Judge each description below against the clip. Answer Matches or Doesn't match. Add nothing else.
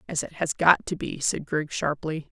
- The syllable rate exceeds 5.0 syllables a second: Doesn't match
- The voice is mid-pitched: Matches